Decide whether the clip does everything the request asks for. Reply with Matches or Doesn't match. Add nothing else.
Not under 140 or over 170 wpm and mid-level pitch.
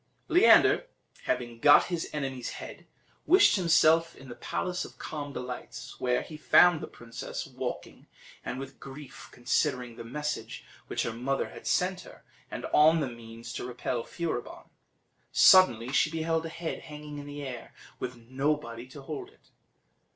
Matches